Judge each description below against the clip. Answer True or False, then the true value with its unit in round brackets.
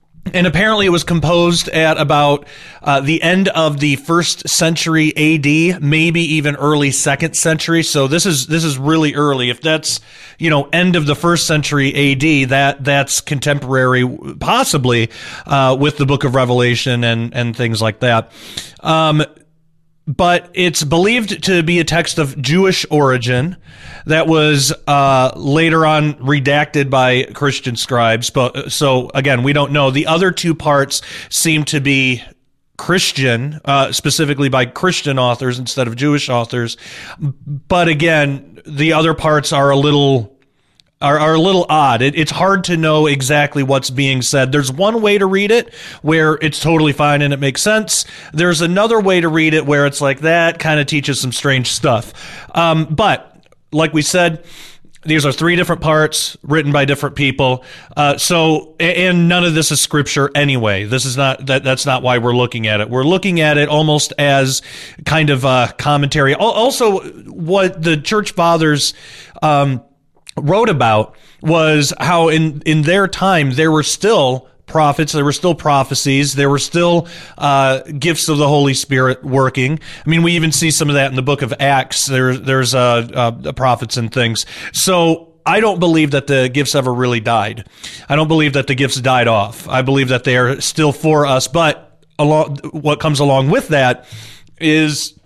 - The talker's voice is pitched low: False (145 Hz)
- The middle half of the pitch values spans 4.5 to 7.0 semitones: False (3.1 semitones)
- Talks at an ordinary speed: True (175 wpm)